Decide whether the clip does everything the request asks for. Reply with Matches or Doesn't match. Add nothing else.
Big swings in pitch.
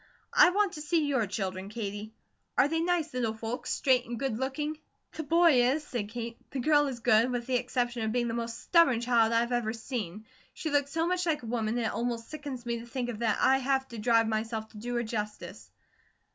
Doesn't match